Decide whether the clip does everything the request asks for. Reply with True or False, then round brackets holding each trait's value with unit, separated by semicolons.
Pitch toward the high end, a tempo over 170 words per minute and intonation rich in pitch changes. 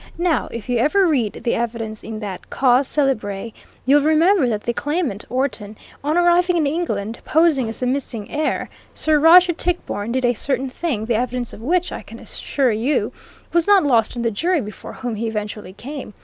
True (255 Hz; 190 wpm; 5.9 semitones)